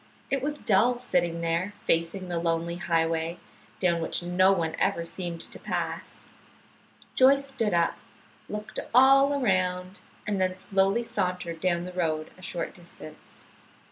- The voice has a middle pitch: Yes, medium, 180 Hz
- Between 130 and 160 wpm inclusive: Yes, average, 140 wpm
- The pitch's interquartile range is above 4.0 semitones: No, average, 3.5 semitones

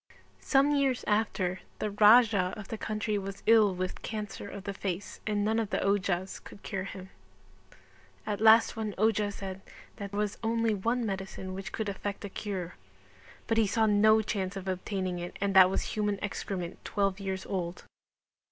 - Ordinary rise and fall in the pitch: No, narrow, 2.2 semitones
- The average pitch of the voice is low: No, high, 200 Hz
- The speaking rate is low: No, average, 180 wpm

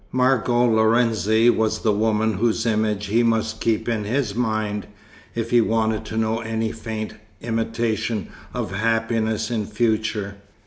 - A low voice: Yes, low, 110 Hz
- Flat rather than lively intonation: Yes, narrow, 1.1 semitones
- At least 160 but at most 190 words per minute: No, average, 140 wpm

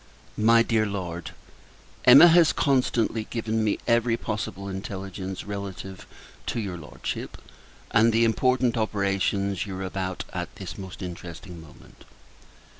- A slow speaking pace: Yes, slow, 125 wpm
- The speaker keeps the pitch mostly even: No, average, 3.4 semitones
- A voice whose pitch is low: Yes, low, 100 Hz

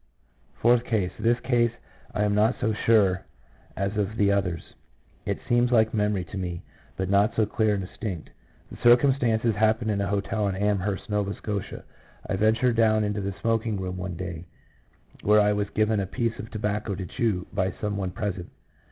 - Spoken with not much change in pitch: Yes, narrow, 2.3 semitones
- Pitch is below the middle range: Yes, low, 105 Hz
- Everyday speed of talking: Yes, average, 185 wpm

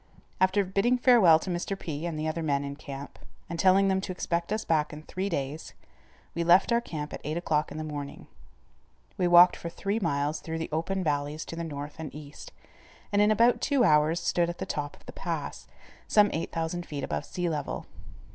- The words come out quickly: Yes, fast, 210 wpm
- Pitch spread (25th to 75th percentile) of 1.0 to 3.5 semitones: No, average, 4.0 semitones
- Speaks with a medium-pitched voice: Yes, medium, 165 Hz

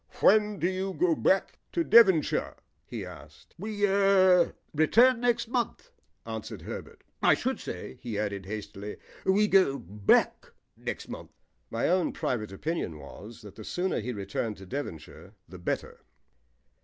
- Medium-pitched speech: Yes, medium, 150 Hz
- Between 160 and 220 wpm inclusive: No, average, 145 wpm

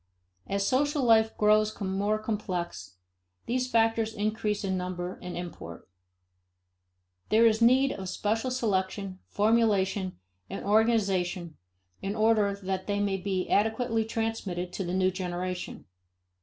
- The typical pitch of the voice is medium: No, high, 205 Hz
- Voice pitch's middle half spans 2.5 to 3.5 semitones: Yes, average, 3.1 semitones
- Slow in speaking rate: Yes, slow, 125 wpm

